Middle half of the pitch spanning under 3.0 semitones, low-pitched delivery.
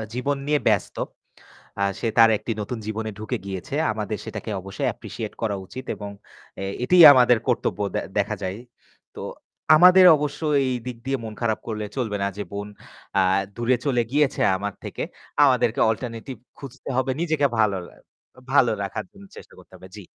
No: average, 4.5 semitones; low, 115 Hz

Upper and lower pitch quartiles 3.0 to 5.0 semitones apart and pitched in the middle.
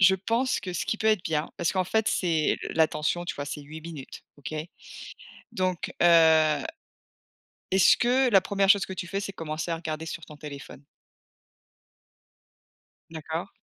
Yes: average, 3.7 semitones; medium, 170 Hz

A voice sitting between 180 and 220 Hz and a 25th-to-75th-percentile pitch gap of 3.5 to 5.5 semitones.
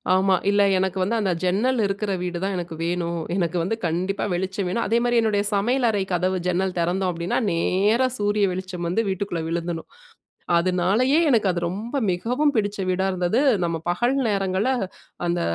No: high, 190 Hz; average, 3.1 semitones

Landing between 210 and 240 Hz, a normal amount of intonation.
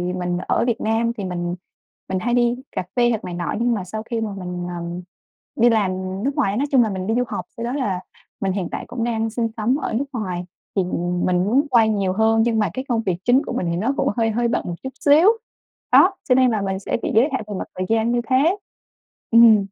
Yes: high, 220 Hz; average, 4.3 semitones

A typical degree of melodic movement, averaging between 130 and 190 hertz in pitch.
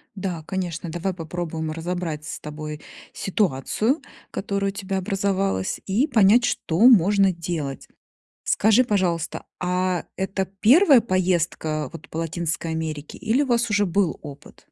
Yes: average, 3.7 semitones; medium, 185 Hz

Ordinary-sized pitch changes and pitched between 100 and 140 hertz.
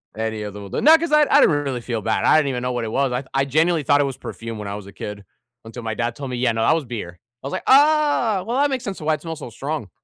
No: wide, 6.3 semitones; low, 135 Hz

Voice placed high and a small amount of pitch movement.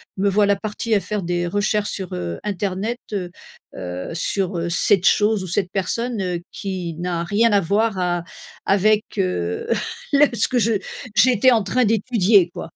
No: high, 195 Hz; average, 3.3 semitones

